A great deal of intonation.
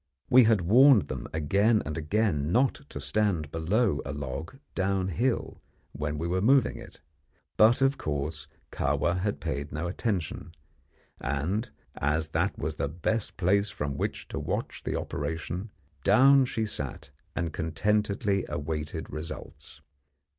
Yes: wide, 5.9 semitones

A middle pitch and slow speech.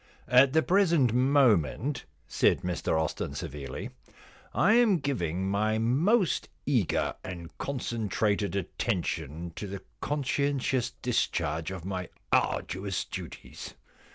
No: low, 110 Hz; slow, 115 wpm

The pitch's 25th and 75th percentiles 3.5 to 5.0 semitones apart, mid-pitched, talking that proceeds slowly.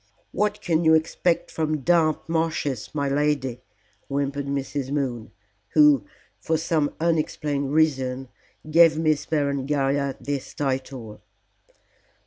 No: average, 2.7 semitones; medium, 145 Hz; slow, 110 wpm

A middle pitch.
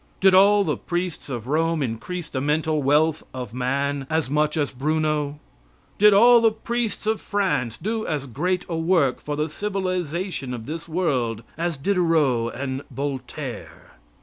Yes: medium, 155 Hz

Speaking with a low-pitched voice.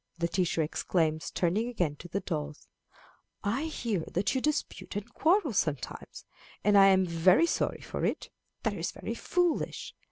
No: high, 190 Hz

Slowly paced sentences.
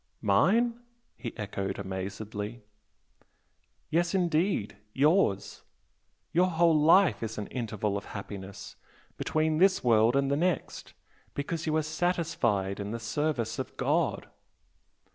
Yes: slow, 120 wpm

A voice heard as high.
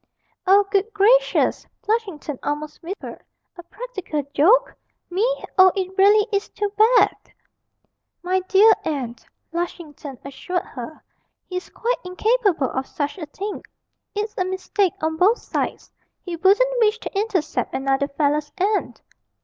Yes: very high, 375 Hz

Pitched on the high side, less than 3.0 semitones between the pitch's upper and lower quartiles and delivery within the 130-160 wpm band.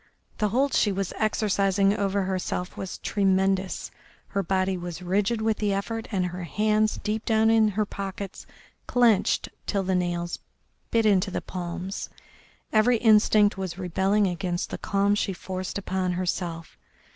Yes: high, 195 Hz; narrow, 2.5 semitones; average, 150 wpm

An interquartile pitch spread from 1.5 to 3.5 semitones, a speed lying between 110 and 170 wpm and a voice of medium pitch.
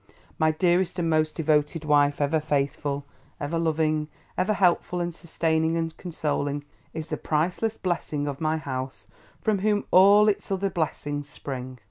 Yes: average, 3.2 semitones; average, 150 wpm; medium, 160 Hz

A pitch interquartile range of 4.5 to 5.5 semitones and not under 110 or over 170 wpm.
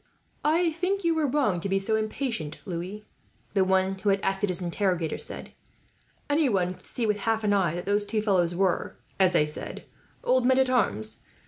No: average, 5.2 semitones; average, 195 wpm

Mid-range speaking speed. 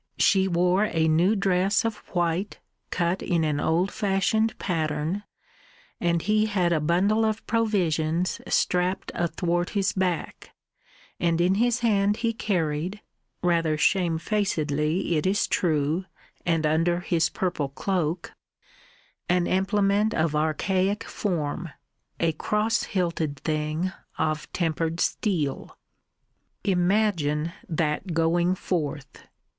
No: slow, 115 wpm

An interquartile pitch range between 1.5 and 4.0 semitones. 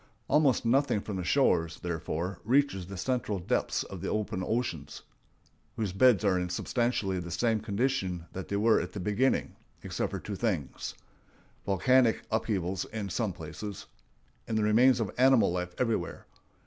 No: average, 4.5 semitones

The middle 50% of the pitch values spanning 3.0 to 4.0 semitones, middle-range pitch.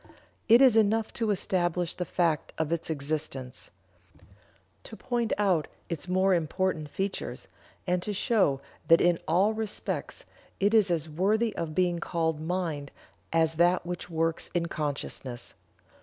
Yes: average, 3.5 semitones; medium, 175 Hz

